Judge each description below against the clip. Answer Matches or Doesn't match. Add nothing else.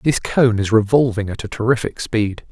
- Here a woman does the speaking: Doesn't match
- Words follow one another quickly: Doesn't match